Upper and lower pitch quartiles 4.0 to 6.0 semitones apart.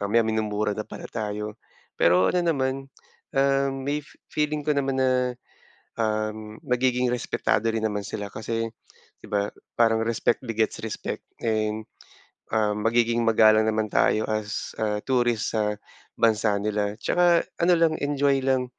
No: average, 3.6 semitones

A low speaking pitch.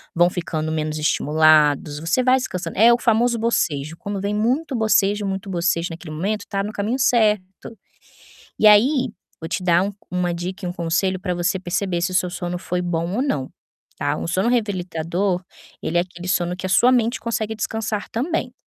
No: medium, 185 Hz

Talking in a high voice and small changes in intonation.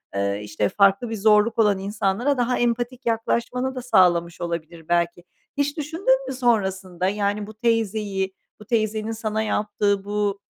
No: high, 210 Hz; average, 3.6 semitones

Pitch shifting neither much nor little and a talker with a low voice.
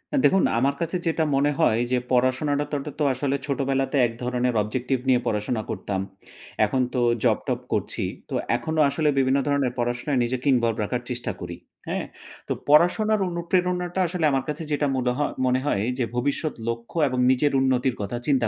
Yes: average, 3.3 semitones; low, 130 Hz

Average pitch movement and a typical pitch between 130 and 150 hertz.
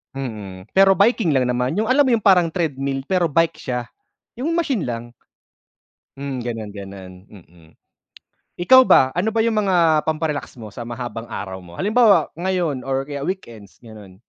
No: wide, 8.4 semitones; medium, 140 Hz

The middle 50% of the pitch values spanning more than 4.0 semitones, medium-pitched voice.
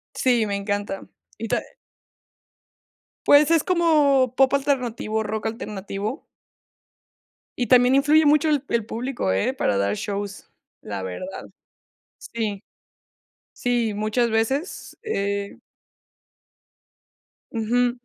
No: average, 4.9 semitones; high, 230 Hz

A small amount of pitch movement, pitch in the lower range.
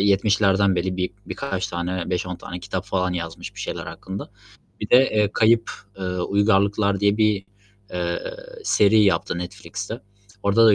Yes: narrow, 2.2 semitones; very low, 95 Hz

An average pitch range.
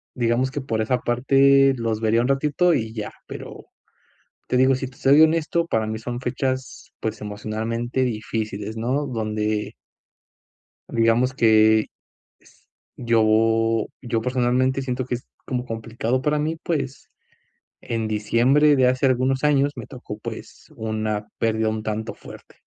Yes: average, 3.2 semitones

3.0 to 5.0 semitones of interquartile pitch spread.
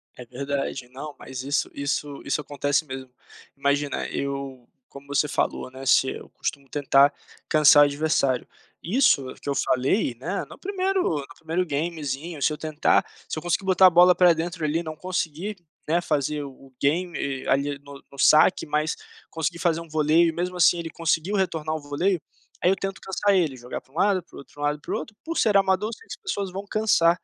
Yes: average, 4.2 semitones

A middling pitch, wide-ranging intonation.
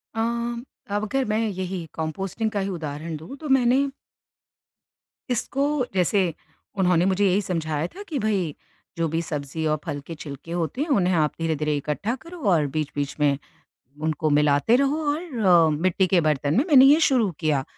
Yes: medium, 180 Hz; wide, 6.4 semitones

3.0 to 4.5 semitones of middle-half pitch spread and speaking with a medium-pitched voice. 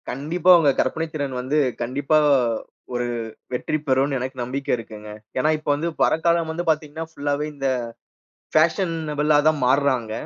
Yes: average, 3.3 semitones; medium, 145 Hz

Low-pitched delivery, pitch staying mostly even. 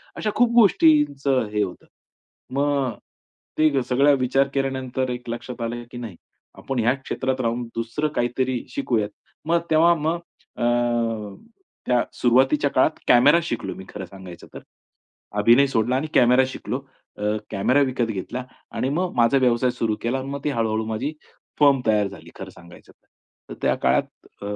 No: low, 125 Hz; average, 3.3 semitones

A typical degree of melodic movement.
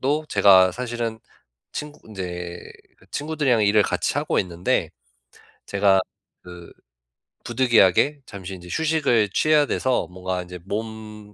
No: wide, 5.7 semitones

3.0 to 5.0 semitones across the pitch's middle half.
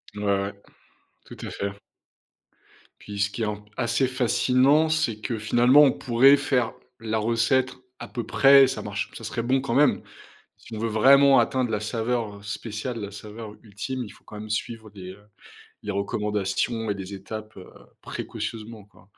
Yes: average, 3.5 semitones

